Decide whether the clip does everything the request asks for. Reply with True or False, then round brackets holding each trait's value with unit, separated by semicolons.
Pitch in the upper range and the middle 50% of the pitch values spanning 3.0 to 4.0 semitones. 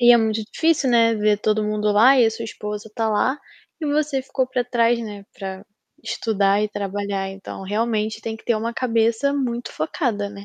False (220 Hz; 2.6 semitones)